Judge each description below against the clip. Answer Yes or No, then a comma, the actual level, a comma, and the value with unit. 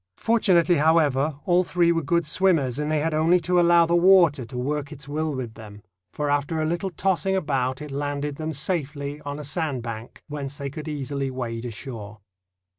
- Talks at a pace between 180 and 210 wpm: Yes, average, 190 wpm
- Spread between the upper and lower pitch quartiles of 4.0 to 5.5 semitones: No, average, 3.6 semitones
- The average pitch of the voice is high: No, medium, 150 Hz